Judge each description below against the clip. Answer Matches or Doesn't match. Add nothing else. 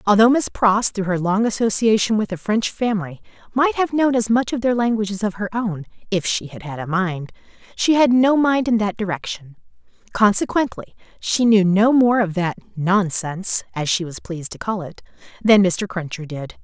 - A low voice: Doesn't match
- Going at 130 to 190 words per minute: Doesn't match